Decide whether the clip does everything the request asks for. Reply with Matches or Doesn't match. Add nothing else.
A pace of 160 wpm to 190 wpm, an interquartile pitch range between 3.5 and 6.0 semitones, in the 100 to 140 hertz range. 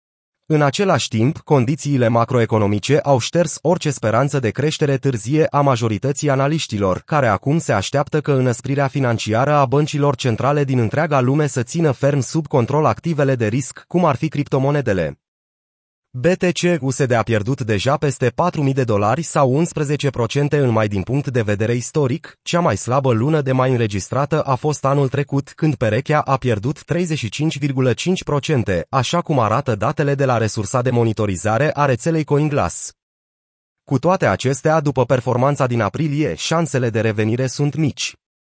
Doesn't match